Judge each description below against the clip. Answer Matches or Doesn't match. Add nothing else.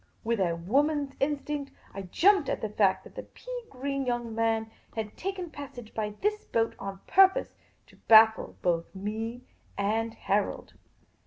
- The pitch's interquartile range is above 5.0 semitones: Matches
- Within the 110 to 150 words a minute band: Doesn't match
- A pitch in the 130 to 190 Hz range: Doesn't match